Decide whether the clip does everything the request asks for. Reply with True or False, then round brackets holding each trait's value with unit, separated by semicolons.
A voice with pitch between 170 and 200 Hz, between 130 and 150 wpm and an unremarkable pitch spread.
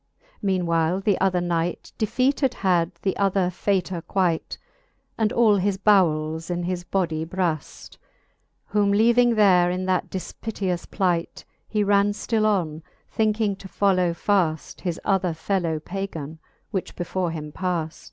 True (185 Hz; 140 wpm; 3.0 semitones)